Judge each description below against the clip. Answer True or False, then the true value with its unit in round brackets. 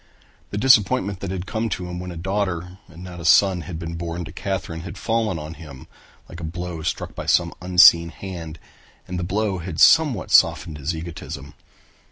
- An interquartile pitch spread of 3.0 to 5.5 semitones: False (2.4 semitones)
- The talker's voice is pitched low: True (90 Hz)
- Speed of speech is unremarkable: True (195 wpm)